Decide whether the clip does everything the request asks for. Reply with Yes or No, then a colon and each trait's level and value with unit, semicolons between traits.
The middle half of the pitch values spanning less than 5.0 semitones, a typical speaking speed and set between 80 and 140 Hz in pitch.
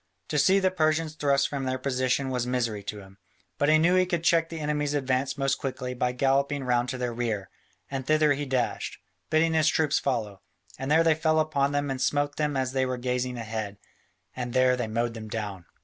No: average, 3.3 semitones; fast, 215 wpm; low, 135 Hz